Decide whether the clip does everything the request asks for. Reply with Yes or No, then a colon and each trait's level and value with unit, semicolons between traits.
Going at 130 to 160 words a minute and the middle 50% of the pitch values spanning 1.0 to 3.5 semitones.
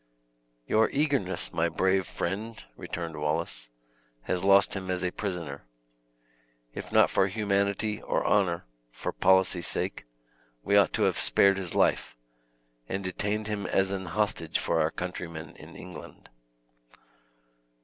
Yes: slow, 135 wpm; average, 3.0 semitones